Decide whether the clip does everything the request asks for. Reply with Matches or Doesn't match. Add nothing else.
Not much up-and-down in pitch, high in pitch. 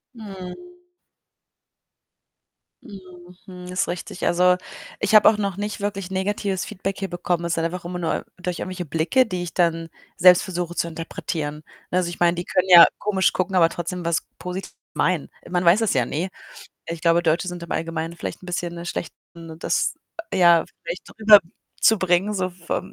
Doesn't match